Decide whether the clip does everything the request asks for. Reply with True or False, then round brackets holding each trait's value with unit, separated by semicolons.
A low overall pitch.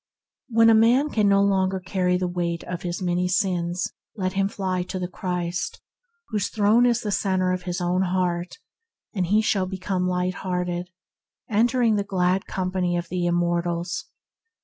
False (185 Hz)